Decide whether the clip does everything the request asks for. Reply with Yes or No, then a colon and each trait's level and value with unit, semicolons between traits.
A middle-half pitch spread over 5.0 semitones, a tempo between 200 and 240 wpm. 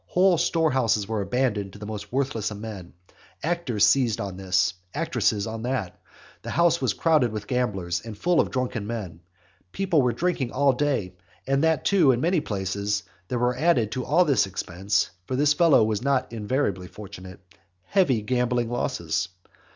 No: wide, 5.4 semitones; average, 170 wpm